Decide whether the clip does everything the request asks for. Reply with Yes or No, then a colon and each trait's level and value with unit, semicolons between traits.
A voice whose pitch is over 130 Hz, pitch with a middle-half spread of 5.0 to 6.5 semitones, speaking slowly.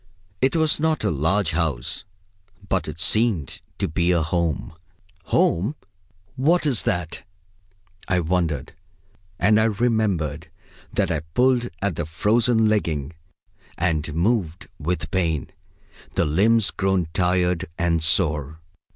No: very low, 90 Hz; average, 5.3 semitones; slow, 125 wpm